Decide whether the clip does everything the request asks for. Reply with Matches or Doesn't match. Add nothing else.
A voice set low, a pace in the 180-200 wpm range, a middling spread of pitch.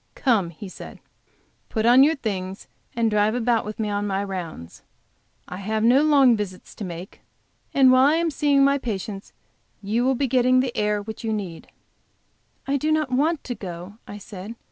Doesn't match